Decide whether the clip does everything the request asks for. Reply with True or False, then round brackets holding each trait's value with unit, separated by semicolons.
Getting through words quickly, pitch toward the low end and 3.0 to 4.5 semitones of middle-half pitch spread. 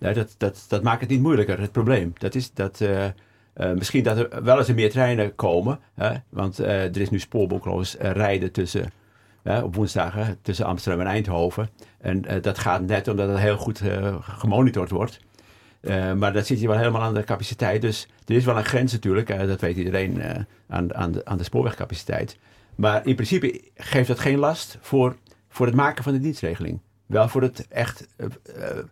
True (205 wpm; 105 Hz; 3.5 semitones)